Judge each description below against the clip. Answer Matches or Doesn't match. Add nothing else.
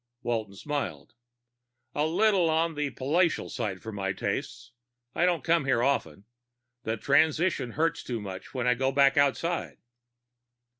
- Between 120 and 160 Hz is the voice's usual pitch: Matches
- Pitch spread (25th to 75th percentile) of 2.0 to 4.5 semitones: Doesn't match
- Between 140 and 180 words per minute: Matches